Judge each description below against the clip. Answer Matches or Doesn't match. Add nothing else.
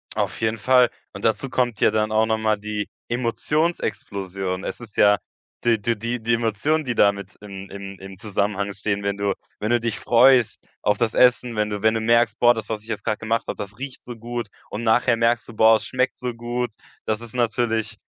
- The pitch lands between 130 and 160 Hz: Doesn't match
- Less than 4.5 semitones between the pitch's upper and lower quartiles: Matches